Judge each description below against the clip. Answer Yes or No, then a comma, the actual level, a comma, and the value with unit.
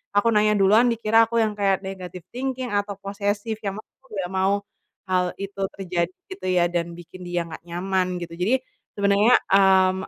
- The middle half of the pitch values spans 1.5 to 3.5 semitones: Yes, narrow, 2.6 semitones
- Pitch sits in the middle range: No, high, 195 Hz